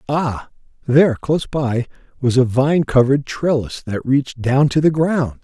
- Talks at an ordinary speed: Yes, average, 165 wpm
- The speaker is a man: Yes, male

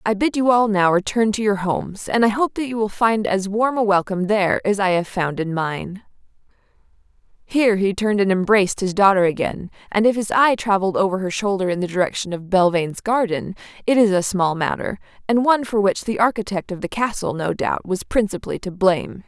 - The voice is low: No, high, 200 Hz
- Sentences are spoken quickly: Yes, fast, 215 wpm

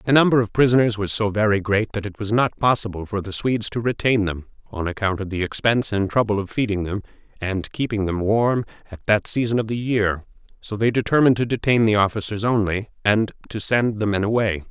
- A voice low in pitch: Yes, low, 105 Hz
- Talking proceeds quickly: Yes, fast, 215 wpm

